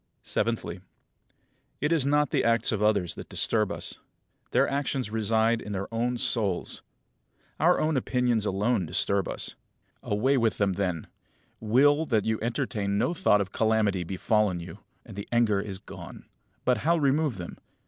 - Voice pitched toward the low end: Yes, low, 110 Hz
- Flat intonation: No, average, 3.9 semitones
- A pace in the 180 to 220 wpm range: No, average, 160 wpm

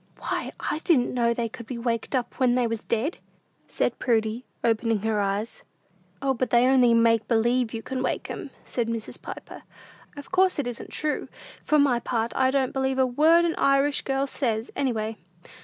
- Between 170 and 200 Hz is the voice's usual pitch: No, high, 245 Hz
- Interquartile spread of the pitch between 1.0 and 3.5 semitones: Yes, average, 2.8 semitones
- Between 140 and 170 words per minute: No, average, 190 wpm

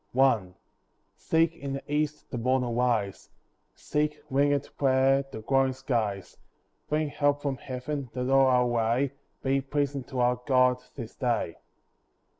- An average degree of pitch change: No, narrow, 2.3 semitones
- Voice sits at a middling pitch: No, low, 130 Hz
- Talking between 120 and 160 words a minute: Yes, average, 140 wpm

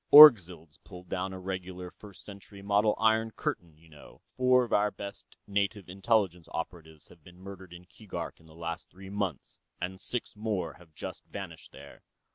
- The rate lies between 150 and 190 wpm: Yes, average, 175 wpm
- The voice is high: No, very low, 95 Hz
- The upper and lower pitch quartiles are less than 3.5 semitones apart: Yes, average, 3.0 semitones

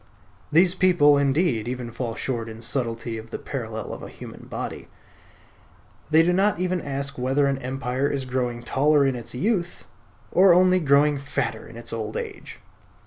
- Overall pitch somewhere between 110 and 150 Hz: Yes, low, 135 Hz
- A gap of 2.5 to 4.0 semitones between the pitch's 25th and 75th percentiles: No, average, 4.8 semitones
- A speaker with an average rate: Yes, average, 170 wpm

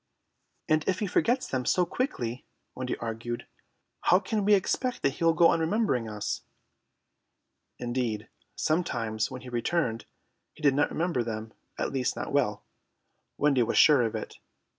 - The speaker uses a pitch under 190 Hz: Yes, low, 135 Hz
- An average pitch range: No, wide, 6.6 semitones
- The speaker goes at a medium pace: Yes, average, 160 wpm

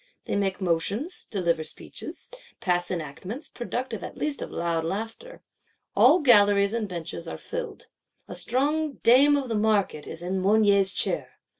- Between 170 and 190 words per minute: No, average, 150 wpm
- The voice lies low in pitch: No, high, 205 Hz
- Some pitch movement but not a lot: No, wide, 6.1 semitones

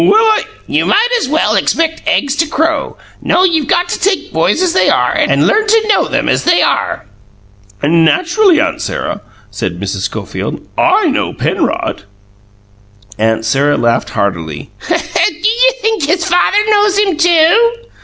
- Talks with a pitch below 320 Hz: No, very high, 330 Hz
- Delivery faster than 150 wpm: Yes, average, 165 wpm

